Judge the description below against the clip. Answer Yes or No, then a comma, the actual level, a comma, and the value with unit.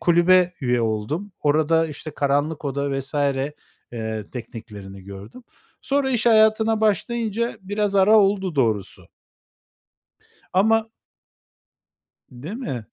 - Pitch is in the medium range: Yes, medium, 160 Hz